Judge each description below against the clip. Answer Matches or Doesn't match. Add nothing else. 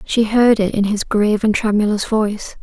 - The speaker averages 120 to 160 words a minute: Doesn't match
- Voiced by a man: Doesn't match